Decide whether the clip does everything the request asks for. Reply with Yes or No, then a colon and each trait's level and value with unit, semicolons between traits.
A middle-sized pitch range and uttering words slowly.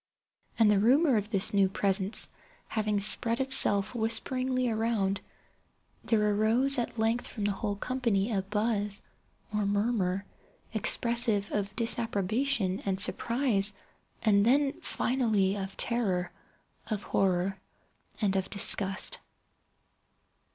Yes: average, 3.1 semitones; slow, 110 wpm